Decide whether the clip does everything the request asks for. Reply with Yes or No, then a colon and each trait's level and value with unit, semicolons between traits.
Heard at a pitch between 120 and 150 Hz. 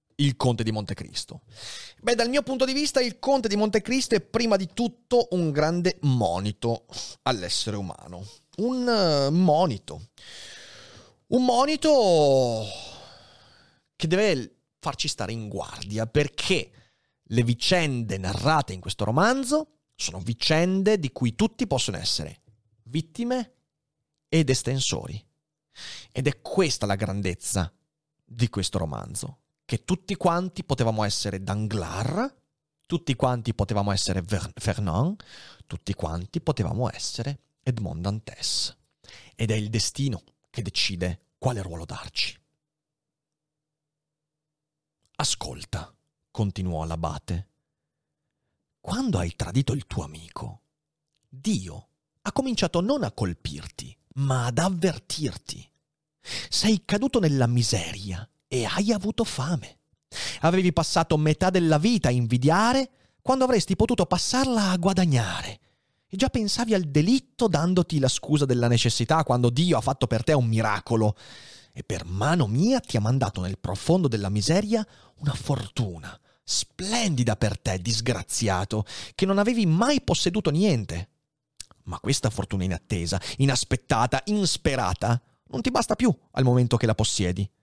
Yes: low, 135 Hz